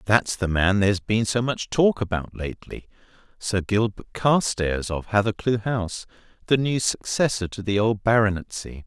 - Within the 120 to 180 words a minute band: Yes, average, 150 wpm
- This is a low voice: Yes, low, 105 Hz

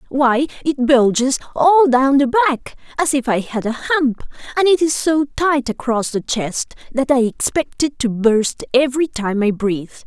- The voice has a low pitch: No, very high, 265 Hz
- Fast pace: No, average, 185 wpm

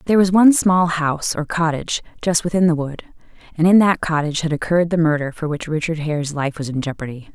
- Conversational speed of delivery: No, fast, 220 wpm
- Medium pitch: Yes, medium, 160 Hz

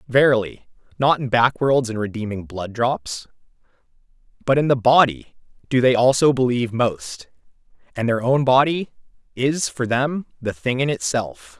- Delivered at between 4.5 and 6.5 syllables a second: Yes, 4.6 syllables/s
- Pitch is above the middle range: No, low, 125 Hz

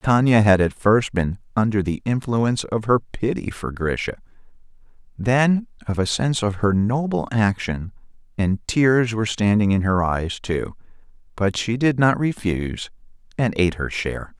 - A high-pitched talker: No, low, 110 Hz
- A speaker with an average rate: Yes, average, 160 wpm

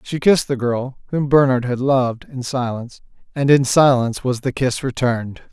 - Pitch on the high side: No, low, 130 Hz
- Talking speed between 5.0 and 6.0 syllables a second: Yes, 5.3 syllables/s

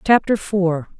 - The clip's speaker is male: No, female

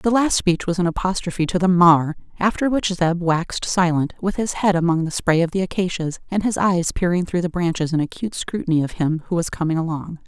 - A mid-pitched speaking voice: Yes, medium, 175 Hz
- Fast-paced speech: Yes, fast, 220 wpm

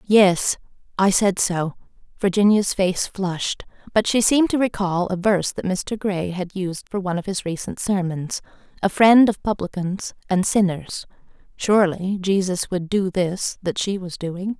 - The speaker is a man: No, female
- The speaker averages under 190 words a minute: Yes, average, 165 wpm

